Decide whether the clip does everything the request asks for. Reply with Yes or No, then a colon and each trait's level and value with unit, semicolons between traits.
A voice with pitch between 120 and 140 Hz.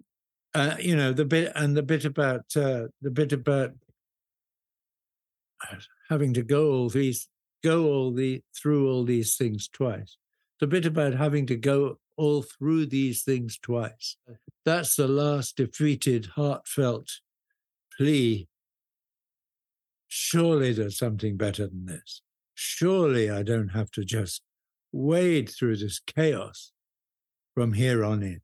Yes: low, 135 Hz